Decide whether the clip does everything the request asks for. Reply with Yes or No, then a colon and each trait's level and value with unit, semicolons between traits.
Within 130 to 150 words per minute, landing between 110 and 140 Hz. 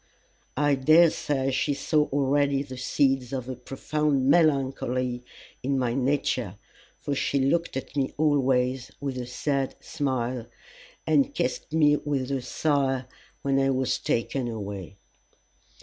Yes: slow, 135 wpm; low, 135 Hz